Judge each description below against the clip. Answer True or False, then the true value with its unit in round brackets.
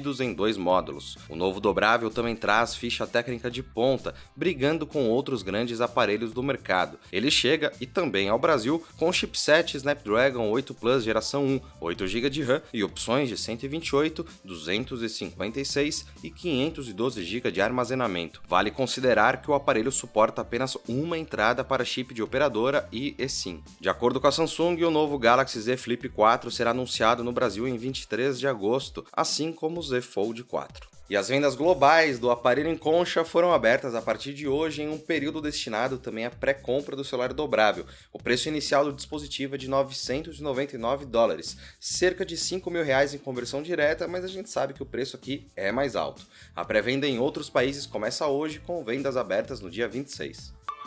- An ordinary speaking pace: True (175 wpm)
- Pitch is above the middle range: False (130 Hz)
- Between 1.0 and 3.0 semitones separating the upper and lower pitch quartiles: False (3.7 semitones)